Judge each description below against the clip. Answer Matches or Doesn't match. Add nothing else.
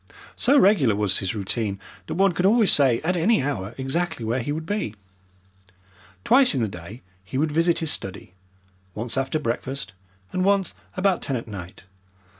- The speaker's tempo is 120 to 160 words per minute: Doesn't match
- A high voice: Doesn't match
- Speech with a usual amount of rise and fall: Doesn't match